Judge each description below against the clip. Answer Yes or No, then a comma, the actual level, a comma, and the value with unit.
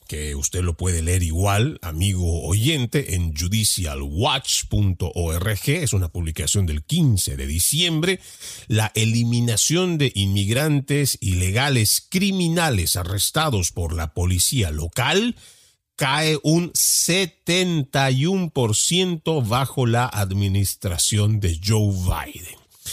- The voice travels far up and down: Yes, wide, 7.9 semitones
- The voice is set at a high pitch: No, low, 105 Hz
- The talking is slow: Yes, slow, 95 wpm